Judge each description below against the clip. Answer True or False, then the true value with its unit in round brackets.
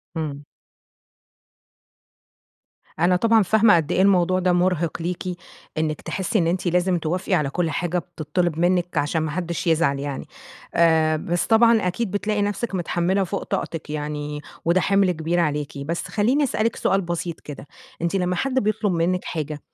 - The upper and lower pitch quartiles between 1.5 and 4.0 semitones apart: True (3.2 semitones)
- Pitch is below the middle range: False (175 Hz)